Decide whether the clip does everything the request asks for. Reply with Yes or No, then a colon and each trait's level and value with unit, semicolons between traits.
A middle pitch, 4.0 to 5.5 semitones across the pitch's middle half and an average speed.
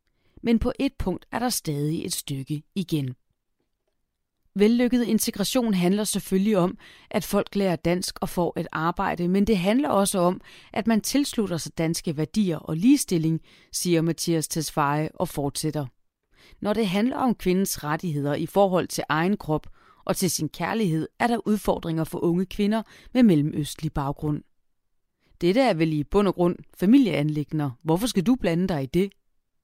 Yes: medium, 180 Hz; average, 4.9 semitones; average, 160 wpm